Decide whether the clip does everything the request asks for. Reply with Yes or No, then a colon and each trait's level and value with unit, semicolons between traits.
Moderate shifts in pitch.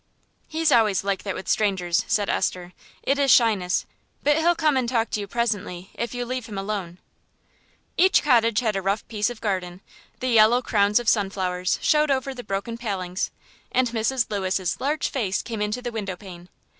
Yes: average, 4.1 semitones